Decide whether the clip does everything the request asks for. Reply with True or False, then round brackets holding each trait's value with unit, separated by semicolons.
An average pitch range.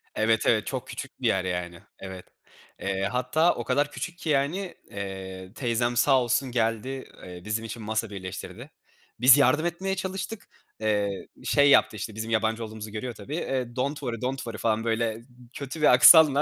True (4.6 semitones)